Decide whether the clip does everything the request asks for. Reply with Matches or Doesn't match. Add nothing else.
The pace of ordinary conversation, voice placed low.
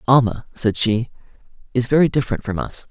Matches